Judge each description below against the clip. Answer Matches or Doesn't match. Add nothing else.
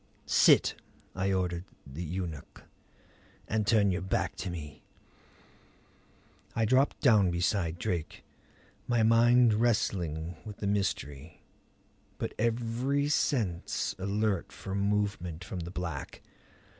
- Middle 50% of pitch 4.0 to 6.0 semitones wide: Matches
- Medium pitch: Doesn't match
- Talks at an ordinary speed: Doesn't match